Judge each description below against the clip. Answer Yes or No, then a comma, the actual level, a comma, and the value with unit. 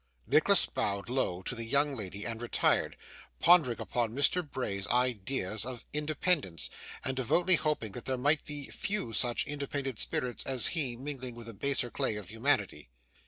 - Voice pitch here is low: Yes, low, 125 Hz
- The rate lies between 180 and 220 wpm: No, average, 165 wpm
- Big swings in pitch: No, average, 4.2 semitones